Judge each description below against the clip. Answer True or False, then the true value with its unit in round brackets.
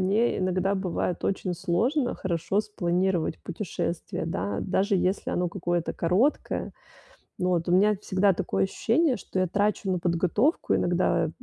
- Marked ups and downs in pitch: False (2.7 semitones)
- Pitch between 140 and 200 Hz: True (185 Hz)